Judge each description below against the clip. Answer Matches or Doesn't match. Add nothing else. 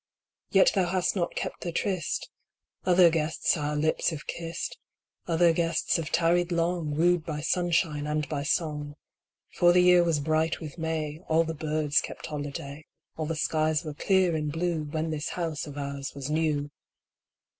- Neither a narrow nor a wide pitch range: Doesn't match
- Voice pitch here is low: Doesn't match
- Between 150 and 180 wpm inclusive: Matches